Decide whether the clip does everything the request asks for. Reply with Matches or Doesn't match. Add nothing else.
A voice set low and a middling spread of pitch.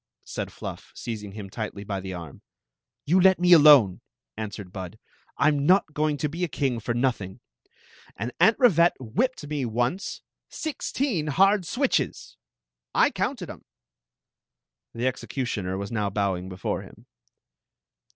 Doesn't match